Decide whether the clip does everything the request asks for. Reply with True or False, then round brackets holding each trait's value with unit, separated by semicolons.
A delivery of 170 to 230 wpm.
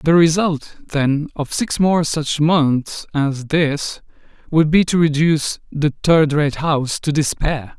False (155 wpm)